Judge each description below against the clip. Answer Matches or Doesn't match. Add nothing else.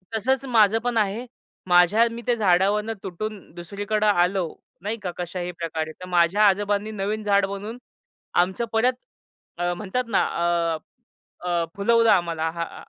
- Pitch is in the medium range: Doesn't match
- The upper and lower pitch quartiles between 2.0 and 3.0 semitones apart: Doesn't match